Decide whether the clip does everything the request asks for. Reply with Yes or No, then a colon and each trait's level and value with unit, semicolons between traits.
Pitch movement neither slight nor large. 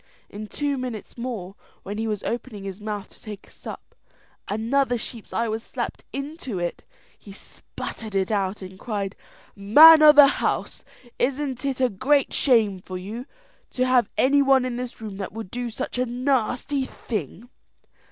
Yes: average, 4.3 semitones